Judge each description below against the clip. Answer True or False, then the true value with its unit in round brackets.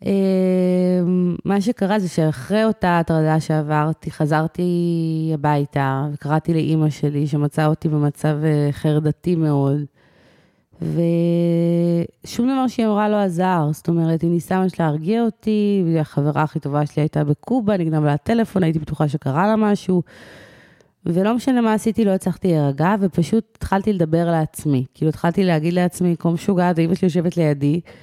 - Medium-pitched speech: True (170 Hz)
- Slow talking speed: False (145 wpm)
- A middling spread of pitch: True (3.5 semitones)